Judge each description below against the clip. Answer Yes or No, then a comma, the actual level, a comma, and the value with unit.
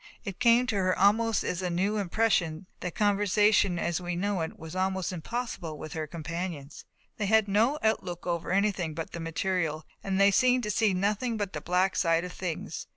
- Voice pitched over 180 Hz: Yes, high, 190 Hz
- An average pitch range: Yes, average, 3.5 semitones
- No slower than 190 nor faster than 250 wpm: Yes, average, 195 wpm